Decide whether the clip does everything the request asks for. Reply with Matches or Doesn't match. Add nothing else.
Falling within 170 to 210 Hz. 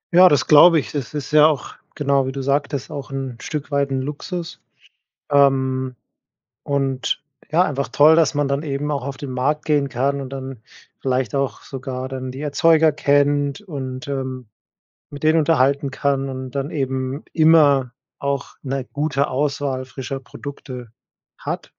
Doesn't match